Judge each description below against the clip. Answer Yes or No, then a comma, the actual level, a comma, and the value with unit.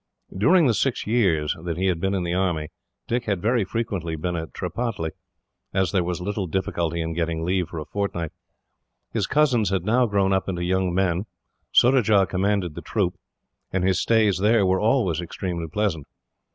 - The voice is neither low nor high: No, very low, 95 Hz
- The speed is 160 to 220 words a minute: Yes, average, 180 wpm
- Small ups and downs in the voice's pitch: No, average, 3.5 semitones